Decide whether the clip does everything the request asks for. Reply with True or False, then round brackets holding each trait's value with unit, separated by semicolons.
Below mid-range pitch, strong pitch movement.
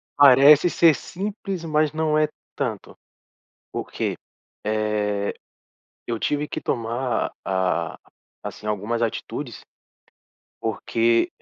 True (120 Hz; 6.1 semitones)